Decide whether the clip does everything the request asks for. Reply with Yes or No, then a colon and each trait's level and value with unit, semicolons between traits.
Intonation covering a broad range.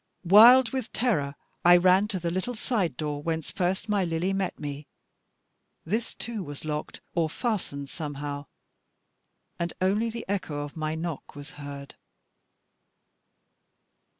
Yes: wide, 5.7 semitones